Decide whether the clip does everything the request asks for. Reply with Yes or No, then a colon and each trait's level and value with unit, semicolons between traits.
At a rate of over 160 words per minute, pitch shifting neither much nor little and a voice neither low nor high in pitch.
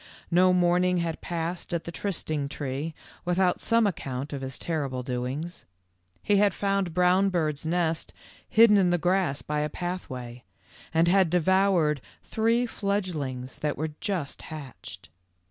No: average, 145 wpm; average, 4.0 semitones; medium, 170 Hz